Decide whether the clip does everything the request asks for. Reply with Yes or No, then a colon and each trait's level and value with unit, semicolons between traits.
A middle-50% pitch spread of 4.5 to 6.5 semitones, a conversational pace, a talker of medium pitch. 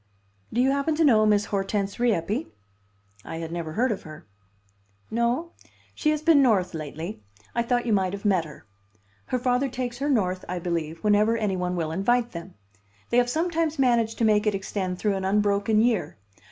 No: average, 5.0 semitones; average, 190 wpm; high, 210 Hz